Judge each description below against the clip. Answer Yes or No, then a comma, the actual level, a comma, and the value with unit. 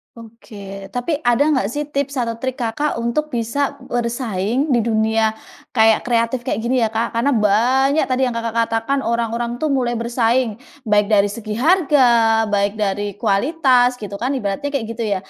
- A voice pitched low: No, high, 235 Hz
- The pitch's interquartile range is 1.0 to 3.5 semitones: Yes, average, 2.9 semitones